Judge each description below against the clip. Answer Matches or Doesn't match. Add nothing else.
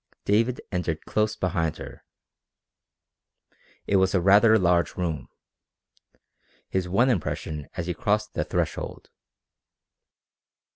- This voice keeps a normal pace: Doesn't match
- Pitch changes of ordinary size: Matches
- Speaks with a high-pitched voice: Doesn't match